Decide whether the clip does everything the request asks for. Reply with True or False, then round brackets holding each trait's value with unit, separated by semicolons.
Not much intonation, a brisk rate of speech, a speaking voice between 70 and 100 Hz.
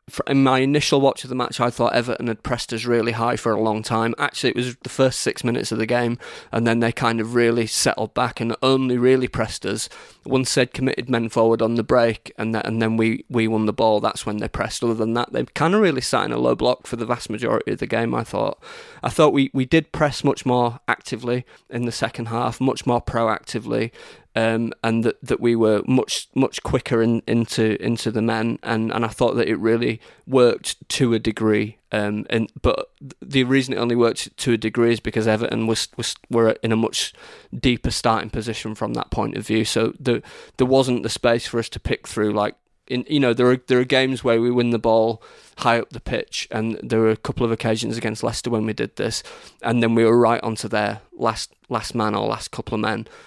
False (1.9 semitones; 235 wpm; 115 Hz)